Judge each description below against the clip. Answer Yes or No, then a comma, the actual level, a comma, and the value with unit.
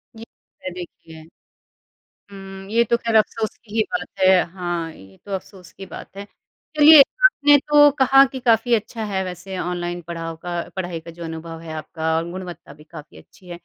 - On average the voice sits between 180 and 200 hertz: Yes, medium, 185 Hz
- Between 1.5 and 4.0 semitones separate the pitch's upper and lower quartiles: No, average, 4.9 semitones